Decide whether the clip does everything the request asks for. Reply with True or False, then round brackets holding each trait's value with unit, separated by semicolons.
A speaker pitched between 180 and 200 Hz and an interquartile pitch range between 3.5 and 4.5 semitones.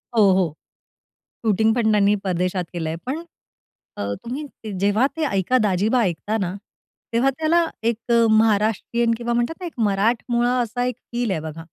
False (220 Hz; 3.8 semitones)